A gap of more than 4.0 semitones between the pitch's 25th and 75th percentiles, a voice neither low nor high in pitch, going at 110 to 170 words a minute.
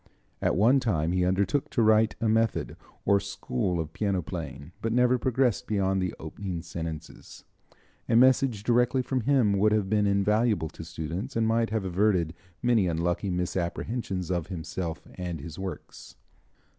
No: average, 4.6 semitones; low, 100 Hz; average, 155 wpm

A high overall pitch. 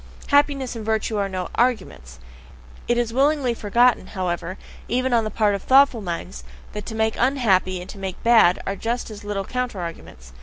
Yes: high, 220 Hz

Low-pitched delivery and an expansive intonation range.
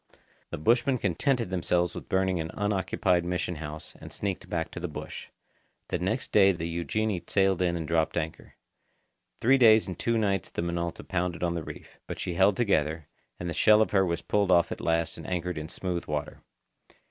No: very low, 90 Hz; average, 3.1 semitones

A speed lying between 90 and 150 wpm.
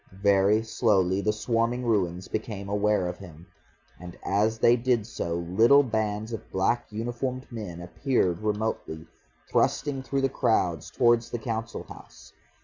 Yes: average, 140 wpm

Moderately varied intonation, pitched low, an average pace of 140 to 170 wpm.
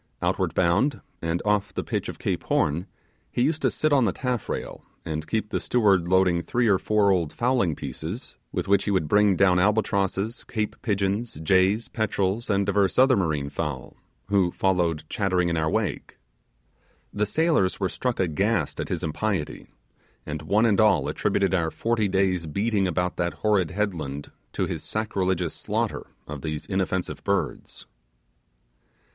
Yes: average, 3.7 semitones; very low, 95 Hz; average, 160 wpm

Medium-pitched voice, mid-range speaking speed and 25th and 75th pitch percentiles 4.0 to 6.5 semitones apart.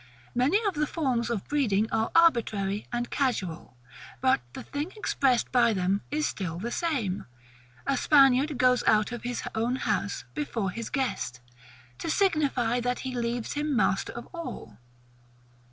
No: high, 245 Hz; average, 155 wpm; average, 4.8 semitones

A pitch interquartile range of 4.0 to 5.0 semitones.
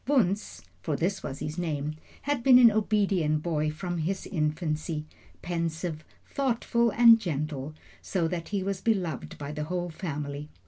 Yes: average, 4.7 semitones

